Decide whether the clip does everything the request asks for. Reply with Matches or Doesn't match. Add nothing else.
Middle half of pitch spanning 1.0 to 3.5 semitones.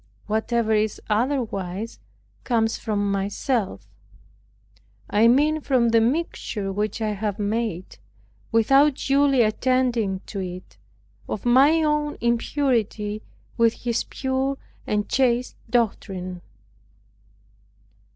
Doesn't match